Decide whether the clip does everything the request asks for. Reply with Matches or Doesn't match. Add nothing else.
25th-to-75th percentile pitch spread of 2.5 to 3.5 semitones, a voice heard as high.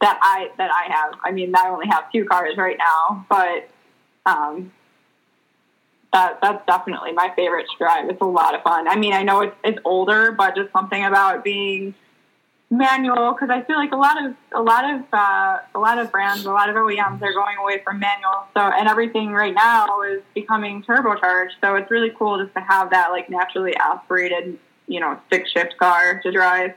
Matches